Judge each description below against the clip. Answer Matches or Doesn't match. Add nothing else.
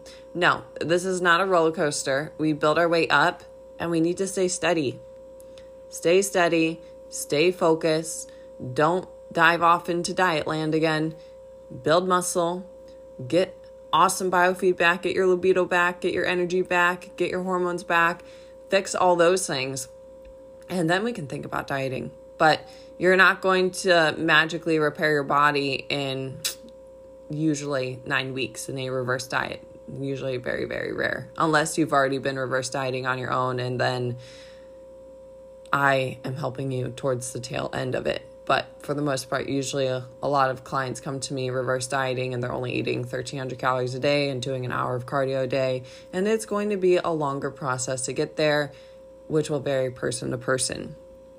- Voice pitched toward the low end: Doesn't match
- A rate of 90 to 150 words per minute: Doesn't match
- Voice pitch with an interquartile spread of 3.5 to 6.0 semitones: Matches